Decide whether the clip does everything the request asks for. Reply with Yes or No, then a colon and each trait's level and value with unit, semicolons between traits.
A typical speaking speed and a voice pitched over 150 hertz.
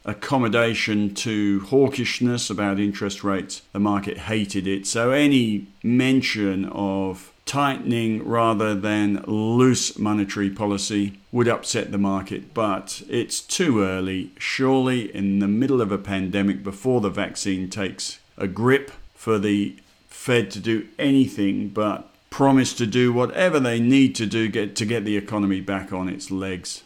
No: average, 145 wpm; low, 105 Hz